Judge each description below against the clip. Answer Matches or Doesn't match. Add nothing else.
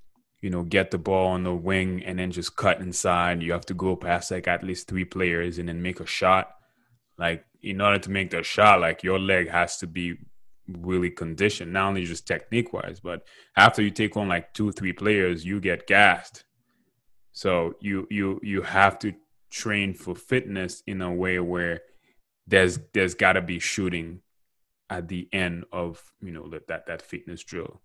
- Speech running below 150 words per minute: Doesn't match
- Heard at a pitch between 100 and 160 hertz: Doesn't match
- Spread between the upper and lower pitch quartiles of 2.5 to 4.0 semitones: Doesn't match